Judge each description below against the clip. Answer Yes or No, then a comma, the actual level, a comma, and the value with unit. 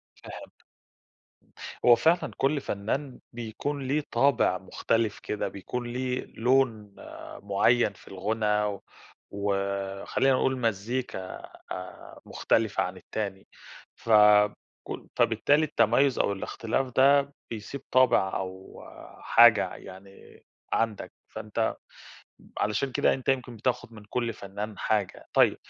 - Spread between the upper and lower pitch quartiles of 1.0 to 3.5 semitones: No, average, 4.3 semitones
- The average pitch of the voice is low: Yes, low, 115 Hz